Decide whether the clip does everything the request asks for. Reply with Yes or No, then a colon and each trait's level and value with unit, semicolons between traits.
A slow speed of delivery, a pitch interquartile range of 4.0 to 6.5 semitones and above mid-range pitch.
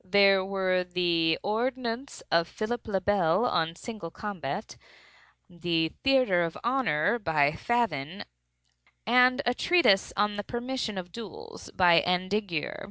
Yes: slow, 125 wpm; wide, 5.6 semitones; high, 195 Hz